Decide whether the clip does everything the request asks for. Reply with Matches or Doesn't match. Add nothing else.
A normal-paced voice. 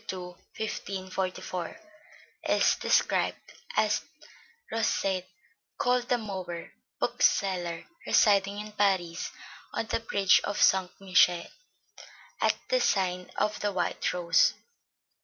Doesn't match